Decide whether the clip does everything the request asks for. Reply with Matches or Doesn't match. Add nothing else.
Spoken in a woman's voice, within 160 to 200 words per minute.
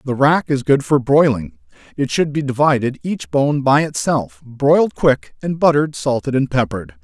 Doesn't match